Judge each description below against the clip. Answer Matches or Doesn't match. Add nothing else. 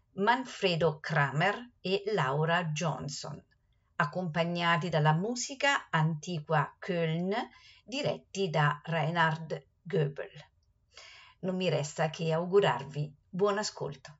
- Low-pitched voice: Doesn't match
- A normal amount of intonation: Matches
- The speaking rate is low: Matches